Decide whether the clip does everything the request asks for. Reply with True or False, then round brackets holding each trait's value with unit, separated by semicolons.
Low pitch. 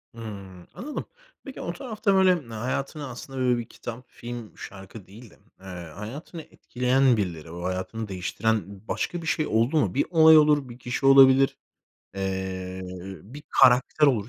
True (120 Hz)